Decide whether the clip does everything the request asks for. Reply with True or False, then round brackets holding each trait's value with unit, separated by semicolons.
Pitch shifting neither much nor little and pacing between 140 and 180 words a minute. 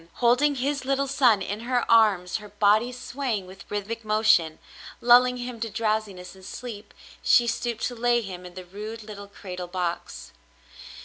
True (3.6 semitones; 165 wpm)